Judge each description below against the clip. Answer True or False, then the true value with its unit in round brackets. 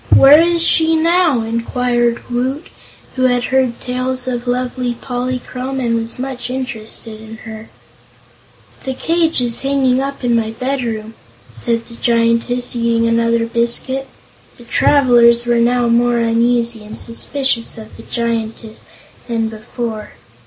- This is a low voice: False (240 Hz)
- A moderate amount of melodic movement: False (1.9 semitones)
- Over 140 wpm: False (135 wpm)